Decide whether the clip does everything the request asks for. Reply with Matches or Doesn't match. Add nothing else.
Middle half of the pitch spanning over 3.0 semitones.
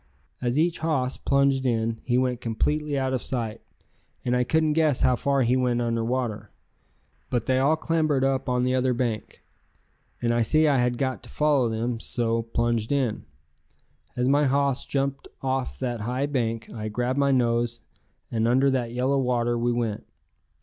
Doesn't match